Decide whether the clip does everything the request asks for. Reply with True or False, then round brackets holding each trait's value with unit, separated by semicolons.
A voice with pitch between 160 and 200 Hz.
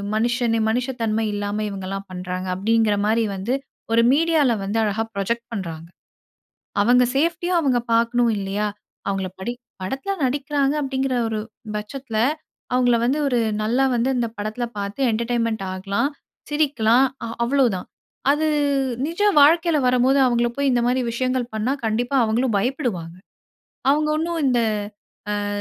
False (235 Hz)